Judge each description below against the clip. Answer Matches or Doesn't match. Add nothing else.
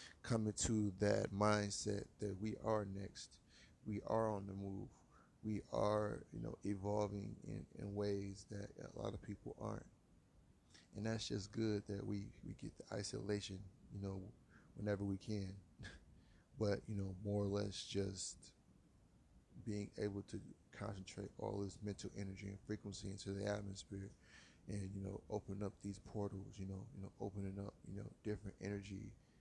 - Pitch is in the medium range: Doesn't match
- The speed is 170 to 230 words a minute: Doesn't match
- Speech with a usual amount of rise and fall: Doesn't match